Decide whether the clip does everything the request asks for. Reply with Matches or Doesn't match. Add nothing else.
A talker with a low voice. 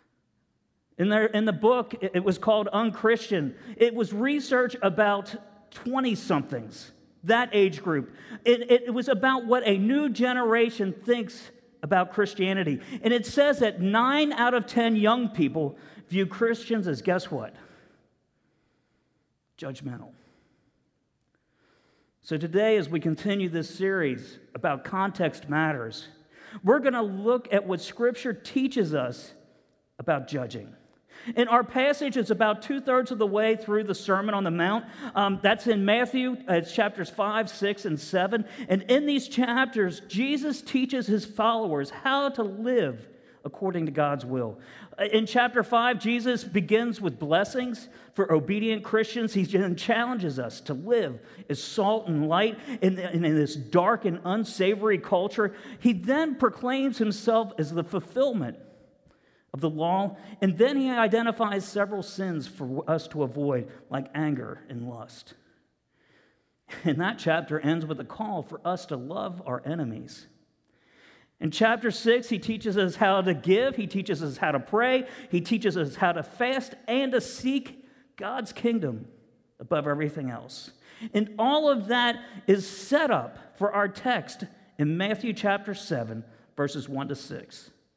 Doesn't match